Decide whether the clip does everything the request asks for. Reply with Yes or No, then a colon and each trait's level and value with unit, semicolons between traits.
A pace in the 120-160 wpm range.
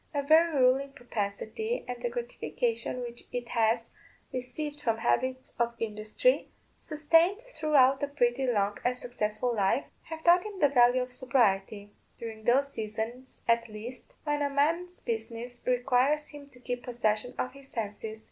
Yes: average, 155 wpm